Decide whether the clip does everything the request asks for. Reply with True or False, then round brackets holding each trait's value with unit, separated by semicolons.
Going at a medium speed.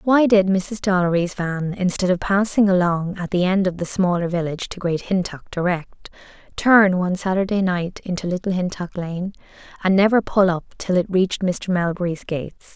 True (180 wpm)